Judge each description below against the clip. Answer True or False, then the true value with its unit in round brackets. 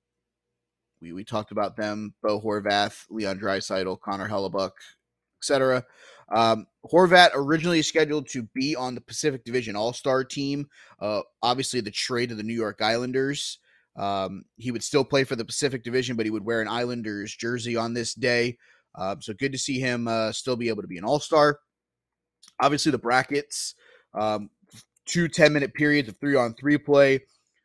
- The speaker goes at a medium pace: True (165 wpm)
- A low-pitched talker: True (120 Hz)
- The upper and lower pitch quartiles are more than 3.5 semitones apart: True (4.6 semitones)